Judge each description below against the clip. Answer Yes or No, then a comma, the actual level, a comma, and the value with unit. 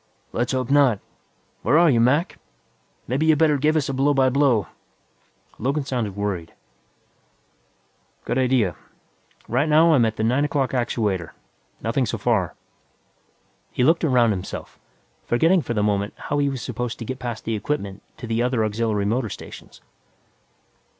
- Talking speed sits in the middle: Yes, average, 155 wpm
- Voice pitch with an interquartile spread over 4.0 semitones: Yes, average, 4.5 semitones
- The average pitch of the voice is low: Yes, low, 125 Hz